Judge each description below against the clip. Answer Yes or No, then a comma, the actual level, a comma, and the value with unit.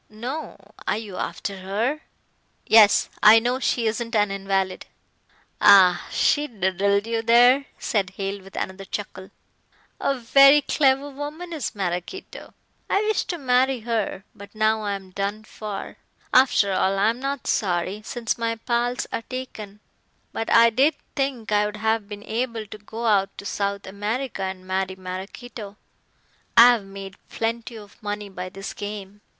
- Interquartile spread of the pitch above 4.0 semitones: No, average, 3.6 semitones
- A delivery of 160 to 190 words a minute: No, average, 145 wpm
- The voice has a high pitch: Yes, high, 215 Hz